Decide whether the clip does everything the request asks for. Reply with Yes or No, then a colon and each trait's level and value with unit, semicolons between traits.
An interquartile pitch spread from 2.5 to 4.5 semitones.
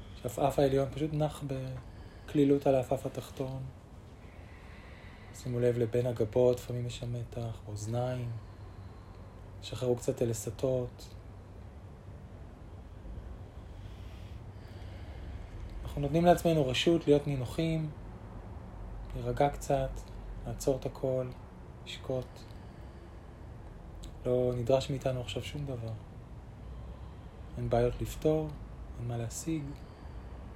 No: average, 5.2 semitones